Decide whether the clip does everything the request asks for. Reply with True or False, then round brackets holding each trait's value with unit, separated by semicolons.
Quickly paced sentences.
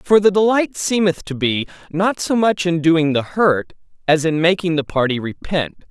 False (195 wpm)